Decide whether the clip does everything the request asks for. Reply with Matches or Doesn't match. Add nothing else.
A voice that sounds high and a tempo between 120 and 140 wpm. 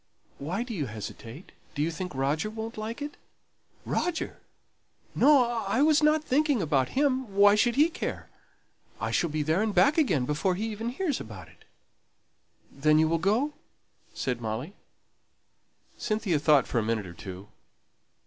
Doesn't match